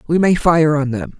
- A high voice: No, medium, 160 Hz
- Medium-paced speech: No, fast, 250 wpm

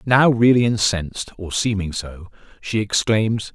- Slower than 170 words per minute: Yes, slow, 135 wpm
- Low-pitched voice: Yes, low, 105 Hz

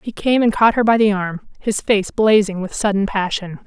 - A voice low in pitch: No, high, 205 Hz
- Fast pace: Yes, fast, 230 wpm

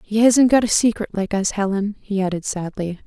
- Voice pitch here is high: Yes, high, 205 Hz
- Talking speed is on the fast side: Yes, fast, 215 wpm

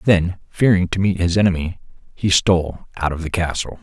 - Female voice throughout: No, male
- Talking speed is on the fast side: No, average, 190 wpm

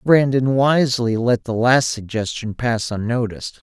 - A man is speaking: Yes, male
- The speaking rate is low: Yes, slow, 130 wpm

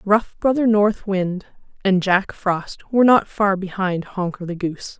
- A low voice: No, high, 195 Hz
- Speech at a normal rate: Yes, average, 170 wpm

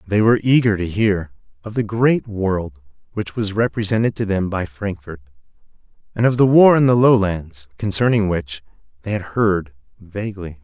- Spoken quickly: No, average, 165 wpm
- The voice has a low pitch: Yes, low, 100 Hz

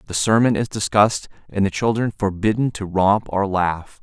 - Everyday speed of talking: Yes, average, 180 wpm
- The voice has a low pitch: Yes, low, 100 Hz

